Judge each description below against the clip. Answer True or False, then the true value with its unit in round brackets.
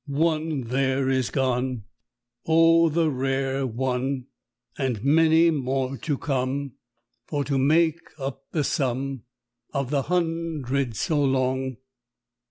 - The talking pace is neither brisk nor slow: False (115 wpm)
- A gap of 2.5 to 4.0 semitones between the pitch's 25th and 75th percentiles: True (3.0 semitones)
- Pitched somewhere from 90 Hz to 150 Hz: True (135 Hz)